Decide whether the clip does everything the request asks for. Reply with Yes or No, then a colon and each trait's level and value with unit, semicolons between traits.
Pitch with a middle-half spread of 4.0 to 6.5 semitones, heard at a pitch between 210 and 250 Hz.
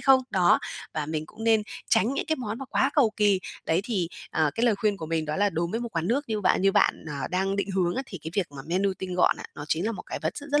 No: average, 5.1 semitones; high, 195 Hz